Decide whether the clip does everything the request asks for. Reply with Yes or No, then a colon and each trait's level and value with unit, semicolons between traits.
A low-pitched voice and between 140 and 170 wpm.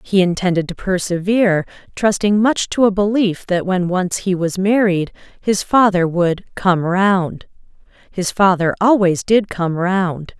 No: high, 190 Hz; average, 150 wpm